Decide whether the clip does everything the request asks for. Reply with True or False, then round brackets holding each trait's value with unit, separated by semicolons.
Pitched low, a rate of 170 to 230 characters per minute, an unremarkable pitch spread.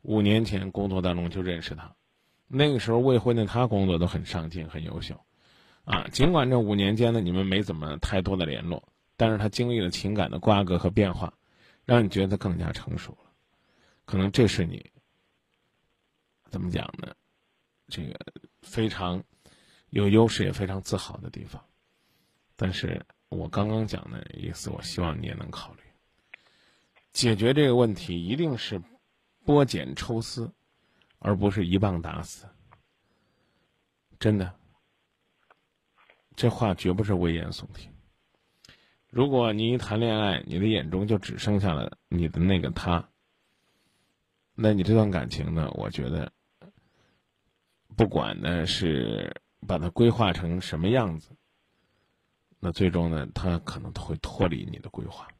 True (100 Hz; 215 characters per minute; 4.1 semitones)